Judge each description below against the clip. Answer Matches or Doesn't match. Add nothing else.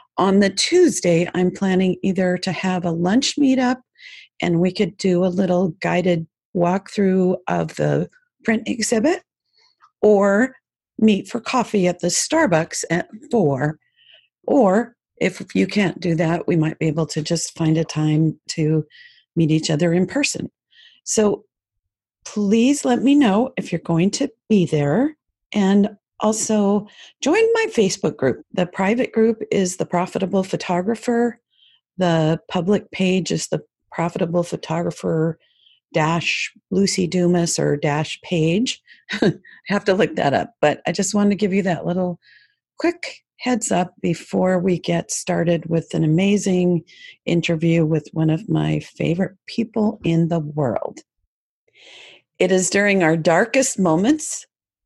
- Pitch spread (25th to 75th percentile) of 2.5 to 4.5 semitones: Doesn't match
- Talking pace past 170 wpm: Doesn't match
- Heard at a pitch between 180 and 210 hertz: Matches